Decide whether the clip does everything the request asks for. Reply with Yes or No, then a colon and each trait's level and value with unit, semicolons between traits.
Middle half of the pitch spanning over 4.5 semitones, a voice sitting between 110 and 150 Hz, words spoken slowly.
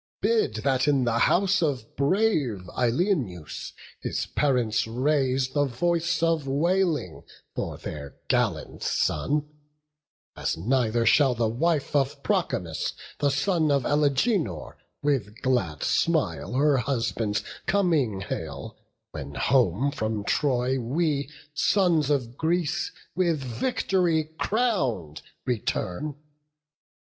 Yes: wide, 5.4 semitones; low, 135 Hz; slow, 110 wpm